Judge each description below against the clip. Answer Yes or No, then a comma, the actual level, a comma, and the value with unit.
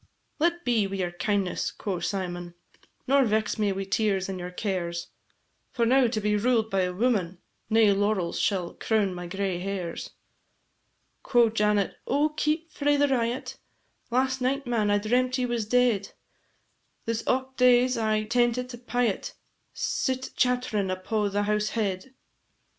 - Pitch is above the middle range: Yes, high, 215 Hz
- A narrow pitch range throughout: No, average, 4.3 semitones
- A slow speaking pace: No, average, 155 wpm